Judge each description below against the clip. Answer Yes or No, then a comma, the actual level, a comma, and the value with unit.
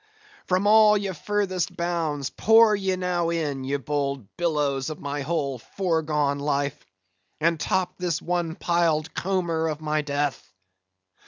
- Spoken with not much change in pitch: No, average, 3.8 semitones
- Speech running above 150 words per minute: No, average, 140 wpm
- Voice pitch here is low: No, medium, 160 Hz